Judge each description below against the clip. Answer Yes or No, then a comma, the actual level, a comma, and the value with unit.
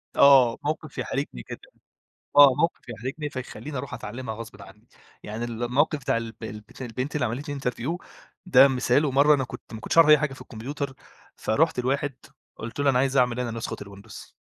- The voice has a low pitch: Yes, low, 130 Hz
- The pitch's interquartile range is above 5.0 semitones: No, average, 3.7 semitones